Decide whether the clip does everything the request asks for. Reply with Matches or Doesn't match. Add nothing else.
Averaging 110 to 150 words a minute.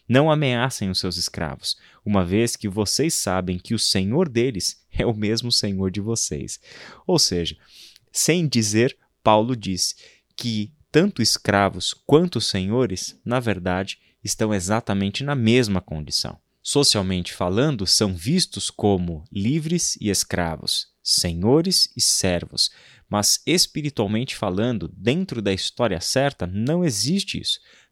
Matches